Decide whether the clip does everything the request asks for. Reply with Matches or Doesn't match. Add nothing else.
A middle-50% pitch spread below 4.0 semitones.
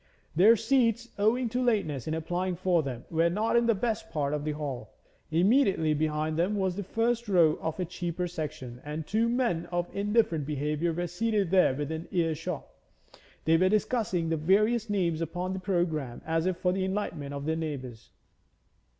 Doesn't match